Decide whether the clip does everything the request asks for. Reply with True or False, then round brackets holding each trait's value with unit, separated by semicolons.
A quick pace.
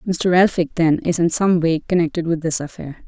True (215 wpm)